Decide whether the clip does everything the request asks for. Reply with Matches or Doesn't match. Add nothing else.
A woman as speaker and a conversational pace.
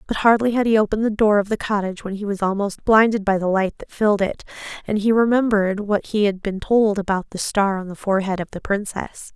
Doesn't match